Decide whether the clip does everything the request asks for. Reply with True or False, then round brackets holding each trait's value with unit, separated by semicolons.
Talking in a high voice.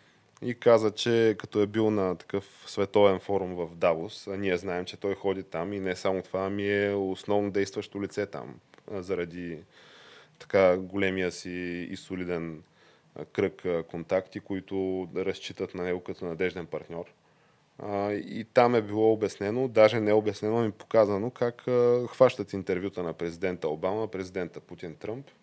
False (100 Hz)